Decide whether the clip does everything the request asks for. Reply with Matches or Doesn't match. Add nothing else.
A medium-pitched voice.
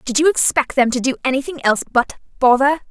Doesn't match